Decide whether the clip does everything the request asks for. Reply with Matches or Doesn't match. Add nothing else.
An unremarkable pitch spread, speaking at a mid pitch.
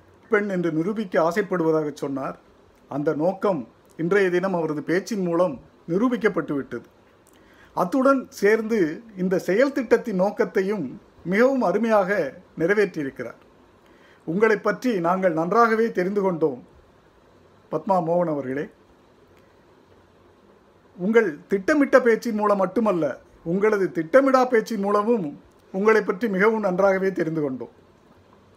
Doesn't match